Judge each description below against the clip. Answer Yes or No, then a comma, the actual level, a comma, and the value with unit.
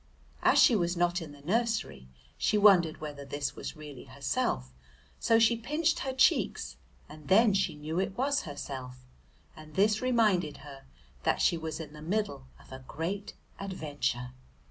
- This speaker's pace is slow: No, average, 165 wpm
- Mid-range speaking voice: Yes, medium, 165 Hz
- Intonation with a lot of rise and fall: Yes, wide, 6.5 semitones